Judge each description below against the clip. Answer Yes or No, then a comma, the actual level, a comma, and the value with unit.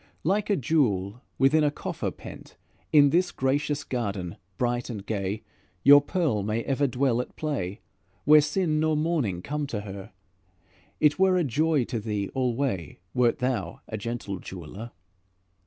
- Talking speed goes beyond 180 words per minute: No, average, 155 wpm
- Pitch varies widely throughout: Yes, wide, 6.2 semitones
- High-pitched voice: No, low, 125 Hz